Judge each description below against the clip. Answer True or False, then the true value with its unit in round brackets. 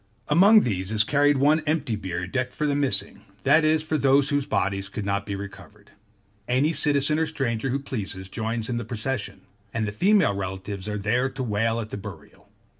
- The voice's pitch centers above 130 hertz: False (115 Hz)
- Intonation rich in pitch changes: True (6.1 semitones)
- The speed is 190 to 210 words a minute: True (195 wpm)